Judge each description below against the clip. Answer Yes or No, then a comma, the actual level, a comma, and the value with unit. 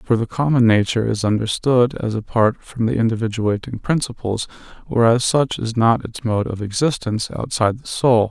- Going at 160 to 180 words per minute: Yes, average, 165 wpm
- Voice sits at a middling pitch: No, low, 115 Hz